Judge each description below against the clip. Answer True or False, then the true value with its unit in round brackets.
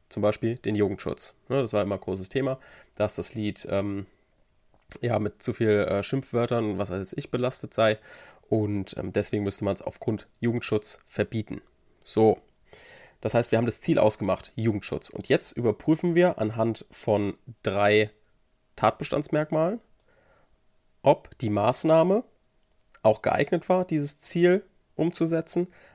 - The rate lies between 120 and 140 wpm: True (135 wpm)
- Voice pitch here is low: True (110 Hz)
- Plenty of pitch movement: True (5.7 semitones)